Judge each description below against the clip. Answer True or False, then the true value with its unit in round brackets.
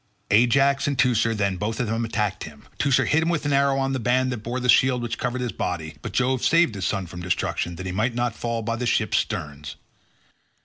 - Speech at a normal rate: False (235 wpm)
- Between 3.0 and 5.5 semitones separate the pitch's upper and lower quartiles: True (4.2 semitones)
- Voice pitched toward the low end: True (120 Hz)